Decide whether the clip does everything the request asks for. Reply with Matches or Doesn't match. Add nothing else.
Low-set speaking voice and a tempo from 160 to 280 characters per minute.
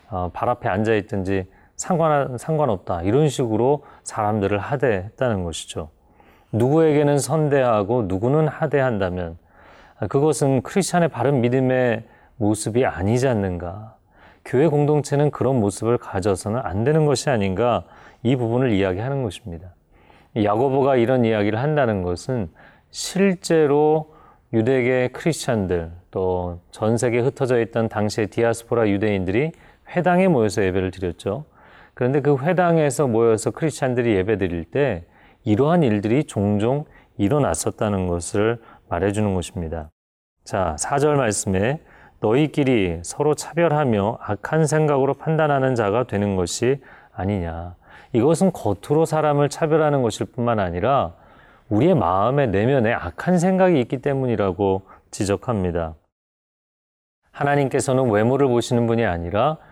Doesn't match